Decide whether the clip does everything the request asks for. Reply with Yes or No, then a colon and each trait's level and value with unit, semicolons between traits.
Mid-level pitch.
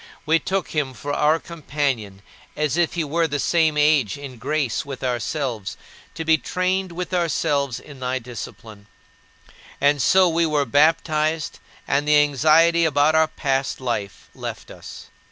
Yes: medium, 150 Hz